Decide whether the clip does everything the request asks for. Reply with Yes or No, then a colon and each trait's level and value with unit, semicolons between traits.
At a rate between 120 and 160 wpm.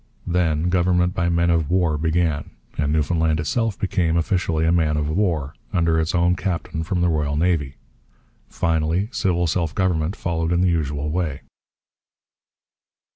Yes: average, 150 wpm